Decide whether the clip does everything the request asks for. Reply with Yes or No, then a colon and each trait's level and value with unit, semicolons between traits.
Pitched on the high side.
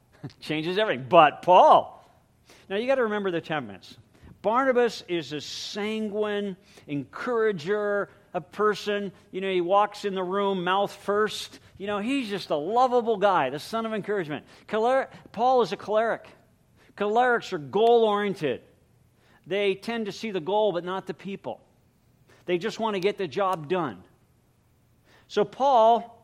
Yes: high, 200 Hz